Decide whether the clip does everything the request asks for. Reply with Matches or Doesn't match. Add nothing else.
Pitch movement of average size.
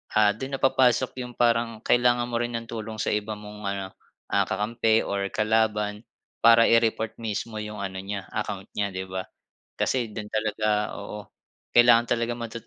Doesn't match